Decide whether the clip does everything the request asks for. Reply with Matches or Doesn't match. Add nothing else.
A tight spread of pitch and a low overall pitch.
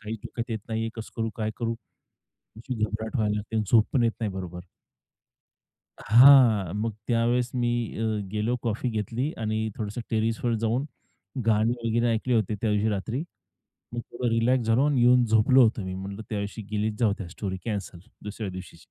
Matches